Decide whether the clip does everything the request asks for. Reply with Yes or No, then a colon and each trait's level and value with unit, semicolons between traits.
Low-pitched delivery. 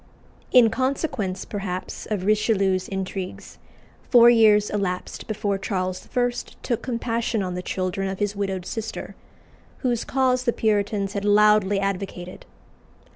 No: high, 205 Hz